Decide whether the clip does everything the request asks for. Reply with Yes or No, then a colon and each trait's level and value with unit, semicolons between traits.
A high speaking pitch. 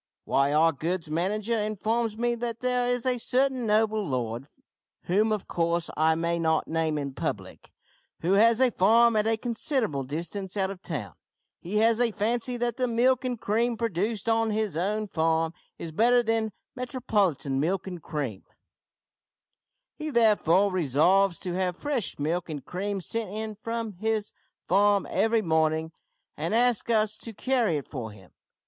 Yes: high, 210 Hz